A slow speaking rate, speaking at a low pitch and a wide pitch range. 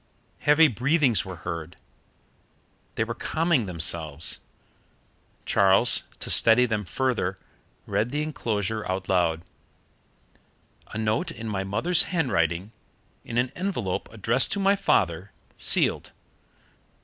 Yes: slow, 115 wpm; low, 110 Hz; wide, 6.3 semitones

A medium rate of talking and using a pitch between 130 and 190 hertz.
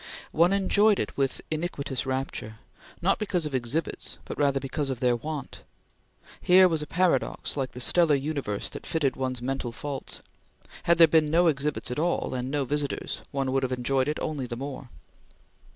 Yes: average, 180 wpm; medium, 140 Hz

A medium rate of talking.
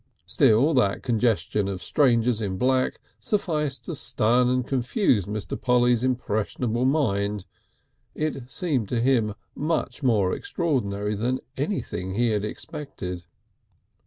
No: slow, 120 wpm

